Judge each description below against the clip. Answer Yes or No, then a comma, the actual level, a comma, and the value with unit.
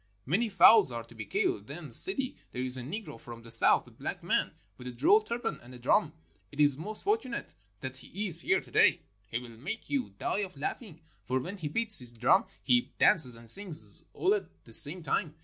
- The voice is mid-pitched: Yes, medium, 150 Hz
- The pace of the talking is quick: Yes, fast, 220 wpm